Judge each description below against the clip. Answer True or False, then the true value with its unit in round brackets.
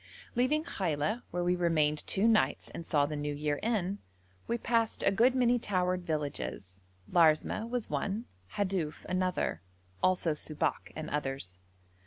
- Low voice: False (180 Hz)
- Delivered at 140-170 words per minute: True (145 wpm)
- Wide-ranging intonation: True (6.4 semitones)